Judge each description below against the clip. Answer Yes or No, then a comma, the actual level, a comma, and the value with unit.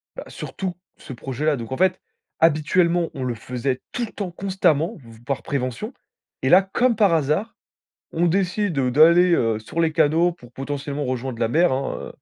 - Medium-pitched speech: Yes, medium, 155 Hz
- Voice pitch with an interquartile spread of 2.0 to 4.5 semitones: No, wide, 5.4 semitones